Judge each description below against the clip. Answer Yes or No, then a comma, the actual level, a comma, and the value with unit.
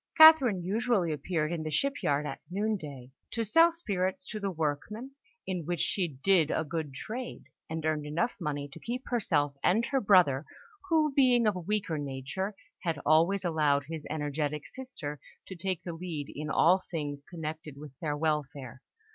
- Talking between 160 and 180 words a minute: Yes, average, 170 wpm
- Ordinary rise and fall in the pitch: No, wide, 5.9 semitones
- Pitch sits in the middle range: Yes, medium, 165 Hz